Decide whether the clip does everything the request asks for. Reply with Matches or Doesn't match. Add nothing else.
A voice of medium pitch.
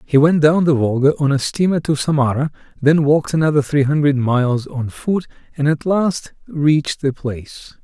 Matches